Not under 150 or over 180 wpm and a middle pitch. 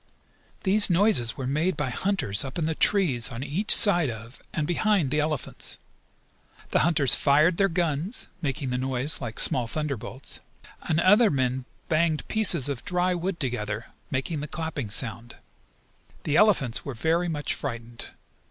Yes: average, 160 wpm; medium, 150 Hz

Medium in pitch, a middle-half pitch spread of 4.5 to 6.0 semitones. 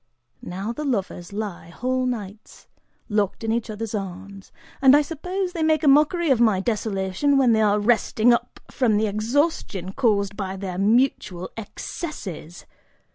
No: high, 220 Hz; average, 5.1 semitones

